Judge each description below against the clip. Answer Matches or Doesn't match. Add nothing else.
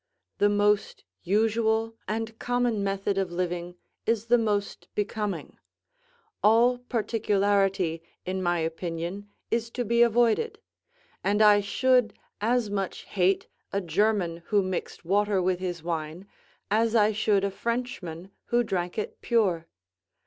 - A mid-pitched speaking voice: Doesn't match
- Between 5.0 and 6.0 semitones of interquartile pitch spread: Doesn't match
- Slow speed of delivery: Matches